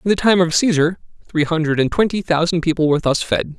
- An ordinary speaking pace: No, fast, 235 wpm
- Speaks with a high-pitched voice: No, medium, 170 Hz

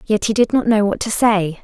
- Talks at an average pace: No, fast, 295 wpm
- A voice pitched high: Yes, high, 210 Hz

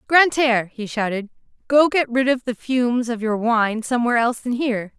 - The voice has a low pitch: No, high, 240 Hz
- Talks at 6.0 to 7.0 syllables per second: Yes, 6.3 syllables/s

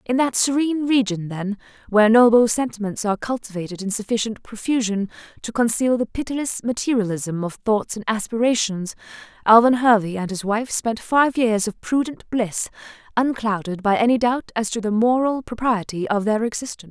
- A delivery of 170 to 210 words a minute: No, average, 160 wpm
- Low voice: No, high, 225 Hz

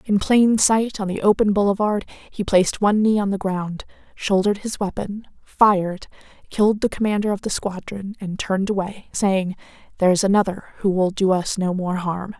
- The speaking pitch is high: Yes, high, 195 Hz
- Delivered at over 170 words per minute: Yes, average, 180 wpm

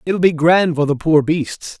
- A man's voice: Yes, male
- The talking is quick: Yes, fast, 235 wpm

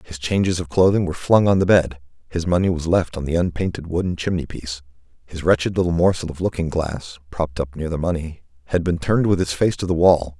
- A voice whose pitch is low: Yes, very low, 85 Hz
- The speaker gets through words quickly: Yes, fast, 230 wpm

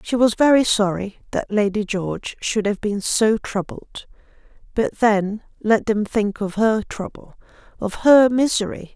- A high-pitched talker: Yes, high, 215 Hz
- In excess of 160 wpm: No, average, 145 wpm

